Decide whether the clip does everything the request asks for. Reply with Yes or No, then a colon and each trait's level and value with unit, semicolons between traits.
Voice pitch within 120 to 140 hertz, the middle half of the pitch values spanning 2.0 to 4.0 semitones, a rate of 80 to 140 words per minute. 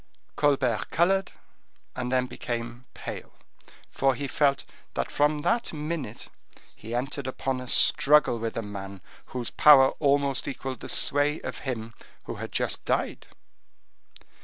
Yes: low, 135 Hz; average, 3.4 semitones; slow, 135 wpm